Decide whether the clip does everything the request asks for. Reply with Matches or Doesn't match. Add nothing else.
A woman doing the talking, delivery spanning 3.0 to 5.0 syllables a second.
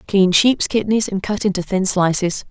Matches